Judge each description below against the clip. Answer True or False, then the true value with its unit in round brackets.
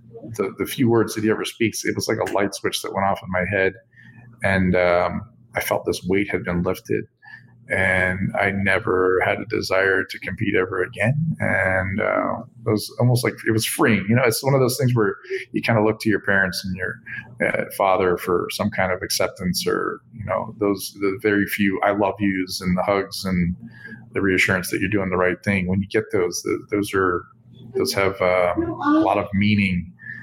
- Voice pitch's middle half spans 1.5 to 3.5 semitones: True (2.9 semitones)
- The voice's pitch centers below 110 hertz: True (100 Hz)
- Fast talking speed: True (215 wpm)